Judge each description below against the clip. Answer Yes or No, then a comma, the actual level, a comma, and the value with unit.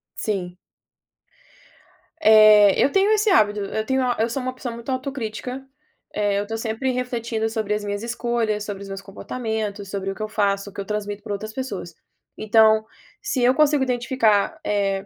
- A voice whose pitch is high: Yes, high, 220 Hz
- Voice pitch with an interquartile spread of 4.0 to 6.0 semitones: No, average, 3.4 semitones